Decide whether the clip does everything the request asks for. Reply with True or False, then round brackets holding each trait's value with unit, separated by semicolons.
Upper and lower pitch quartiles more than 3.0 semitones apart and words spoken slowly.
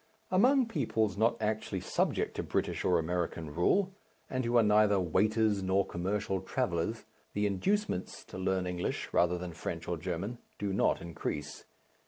False (4.1 semitones; 155 wpm)